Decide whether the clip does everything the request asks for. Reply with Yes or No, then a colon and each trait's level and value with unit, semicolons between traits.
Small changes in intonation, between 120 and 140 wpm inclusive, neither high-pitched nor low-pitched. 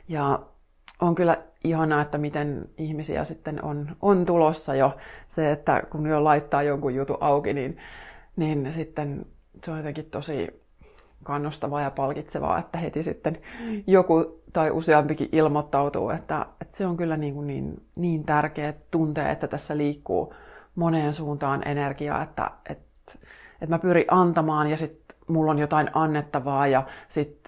No: narrow, 1.8 semitones; average, 150 wpm; medium, 150 Hz